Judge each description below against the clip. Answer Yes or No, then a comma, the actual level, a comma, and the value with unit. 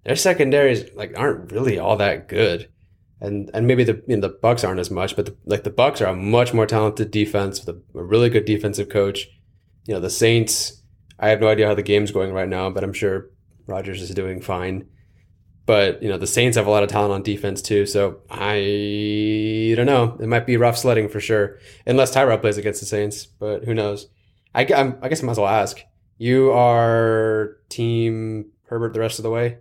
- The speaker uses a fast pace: Yes, fast, 220 wpm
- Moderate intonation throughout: No, narrow, 2.2 semitones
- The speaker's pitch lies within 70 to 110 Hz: Yes, low, 105 Hz